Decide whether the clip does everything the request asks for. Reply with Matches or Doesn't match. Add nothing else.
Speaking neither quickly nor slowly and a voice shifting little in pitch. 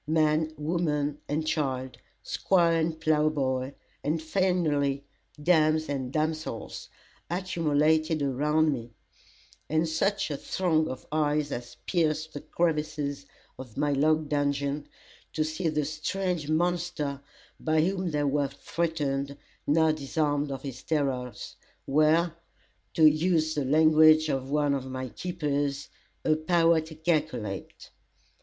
Doesn't match